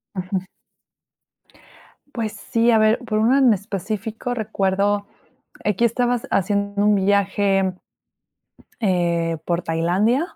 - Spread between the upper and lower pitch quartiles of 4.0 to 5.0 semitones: No, average, 2.8 semitones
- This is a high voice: Yes, high, 205 Hz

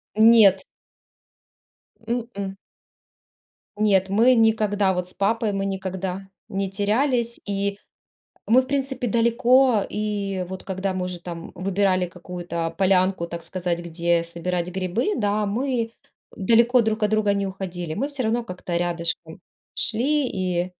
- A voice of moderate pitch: No, high, 195 Hz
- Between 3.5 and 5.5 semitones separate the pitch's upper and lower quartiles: Yes, average, 3.8 semitones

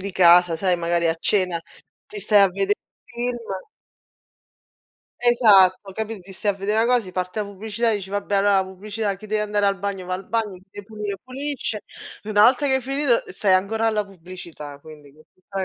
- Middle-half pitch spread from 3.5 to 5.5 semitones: No, average, 2.7 semitones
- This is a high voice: Yes, high, 200 Hz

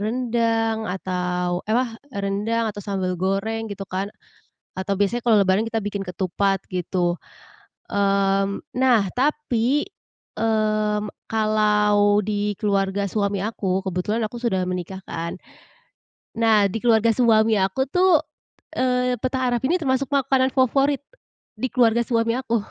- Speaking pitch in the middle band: No, high, 215 Hz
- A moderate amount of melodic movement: Yes, average, 3.2 semitones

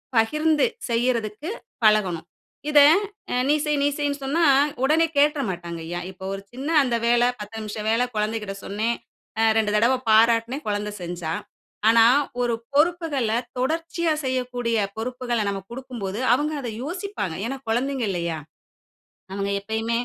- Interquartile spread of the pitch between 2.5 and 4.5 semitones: No, average, 4.9 semitones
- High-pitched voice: Yes, high, 235 Hz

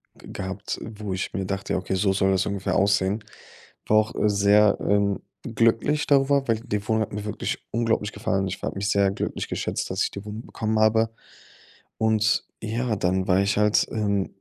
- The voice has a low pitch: Yes, low, 105 Hz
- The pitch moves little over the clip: Yes, narrow, 2.1 semitones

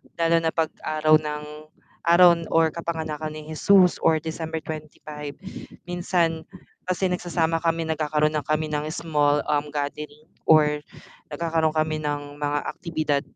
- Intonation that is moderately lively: No, narrow, 1.6 semitones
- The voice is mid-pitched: Yes, medium, 155 Hz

